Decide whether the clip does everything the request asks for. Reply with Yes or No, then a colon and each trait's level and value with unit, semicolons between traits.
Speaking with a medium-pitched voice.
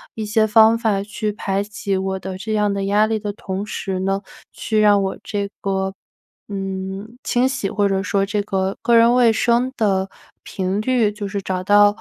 No: high, 205 Hz